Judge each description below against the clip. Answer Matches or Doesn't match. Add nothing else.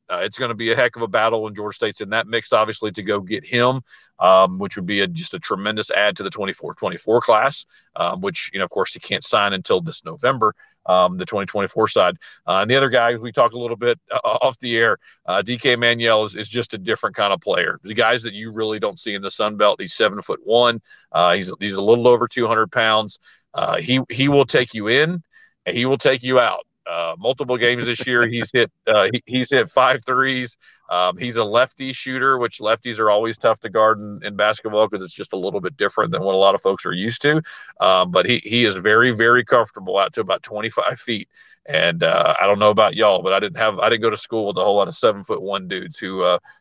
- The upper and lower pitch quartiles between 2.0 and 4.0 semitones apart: Matches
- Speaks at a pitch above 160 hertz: Doesn't match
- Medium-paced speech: Doesn't match